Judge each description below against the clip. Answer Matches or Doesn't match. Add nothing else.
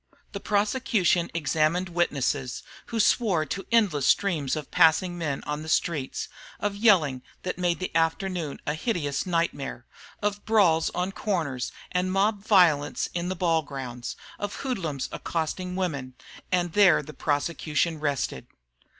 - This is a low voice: Doesn't match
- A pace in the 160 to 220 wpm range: Doesn't match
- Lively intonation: Doesn't match